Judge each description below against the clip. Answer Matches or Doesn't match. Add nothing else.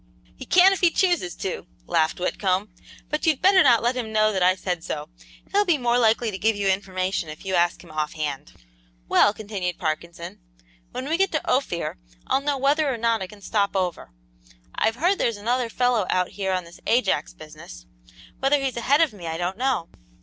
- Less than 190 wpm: Doesn't match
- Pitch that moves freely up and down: Matches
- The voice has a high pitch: Matches